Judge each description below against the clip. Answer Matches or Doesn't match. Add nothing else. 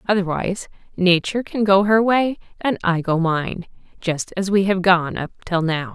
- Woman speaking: Matches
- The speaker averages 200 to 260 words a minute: Doesn't match